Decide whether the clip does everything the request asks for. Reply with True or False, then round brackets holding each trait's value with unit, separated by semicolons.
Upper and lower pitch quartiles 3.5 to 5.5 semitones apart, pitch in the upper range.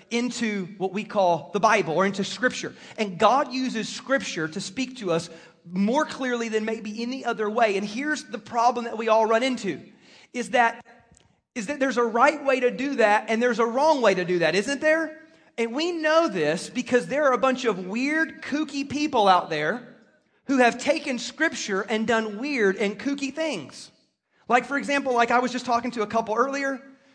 True (4.3 semitones; 240 Hz)